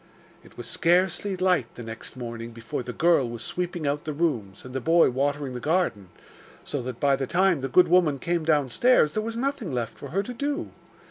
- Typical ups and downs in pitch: No, wide, 6.3 semitones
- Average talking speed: No, fast, 210 wpm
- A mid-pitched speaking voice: Yes, medium, 150 Hz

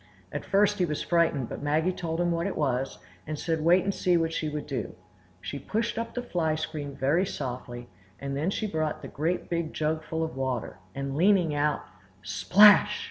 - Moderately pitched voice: Yes, medium, 160 Hz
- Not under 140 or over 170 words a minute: No, average, 195 wpm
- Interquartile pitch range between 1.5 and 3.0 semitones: No, average, 4.3 semitones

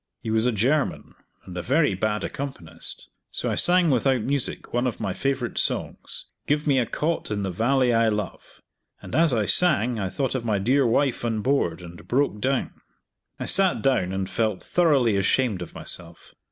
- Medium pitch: No, low, 120 Hz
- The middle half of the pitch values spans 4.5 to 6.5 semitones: Yes, average, 5.2 semitones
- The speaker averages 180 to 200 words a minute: Yes, average, 190 wpm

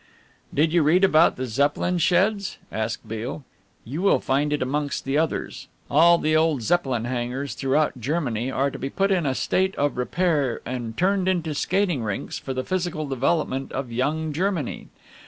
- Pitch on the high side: No, medium, 145 Hz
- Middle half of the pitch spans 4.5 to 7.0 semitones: Yes, average, 4.8 semitones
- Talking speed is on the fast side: No, average, 175 wpm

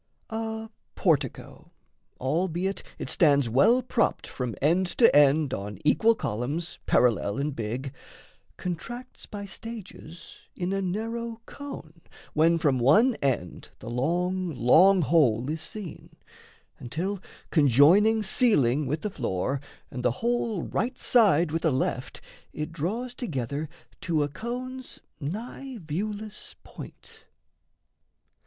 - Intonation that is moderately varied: No, wide, 7.7 semitones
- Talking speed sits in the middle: No, slow, 120 wpm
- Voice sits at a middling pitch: Yes, medium, 170 Hz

